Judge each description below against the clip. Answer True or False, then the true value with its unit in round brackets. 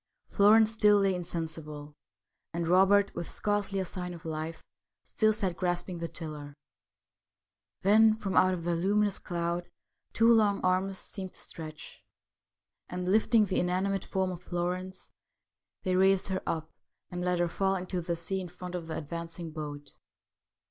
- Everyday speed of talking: True (155 wpm)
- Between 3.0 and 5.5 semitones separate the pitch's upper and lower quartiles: False (2.5 semitones)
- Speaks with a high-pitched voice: False (180 Hz)